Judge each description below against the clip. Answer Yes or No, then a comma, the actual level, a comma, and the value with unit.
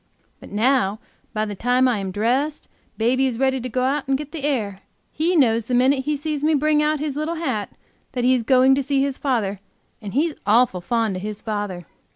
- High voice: Yes, very high, 255 Hz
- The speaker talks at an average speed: No, fast, 220 wpm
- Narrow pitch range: No, average, 4.6 semitones